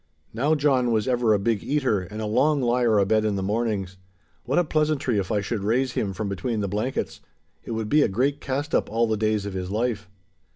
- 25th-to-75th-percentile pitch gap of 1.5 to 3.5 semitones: No, average, 4.0 semitones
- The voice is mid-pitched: No, low, 110 Hz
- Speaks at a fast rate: Yes, fast, 225 wpm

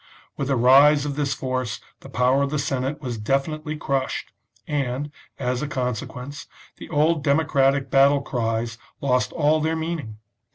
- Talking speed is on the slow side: No, average, 160 wpm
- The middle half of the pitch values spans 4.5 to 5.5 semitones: No, average, 2.8 semitones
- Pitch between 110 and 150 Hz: Yes, medium, 140 Hz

